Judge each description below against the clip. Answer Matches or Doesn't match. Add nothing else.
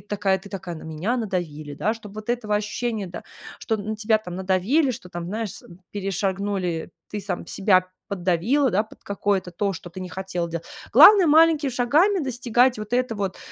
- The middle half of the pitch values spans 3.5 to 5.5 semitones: Matches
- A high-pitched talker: Matches